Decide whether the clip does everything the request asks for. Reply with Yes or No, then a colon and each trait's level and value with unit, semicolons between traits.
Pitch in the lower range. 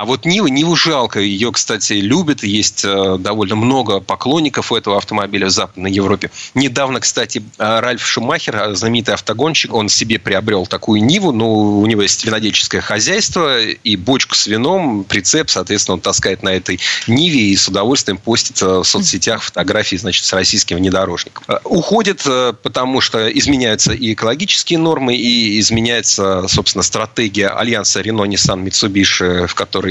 Yes: low, 105 Hz